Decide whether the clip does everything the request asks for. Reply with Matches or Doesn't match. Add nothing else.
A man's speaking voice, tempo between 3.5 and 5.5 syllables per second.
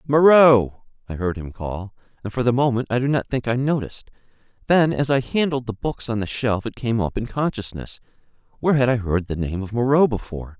Doesn't match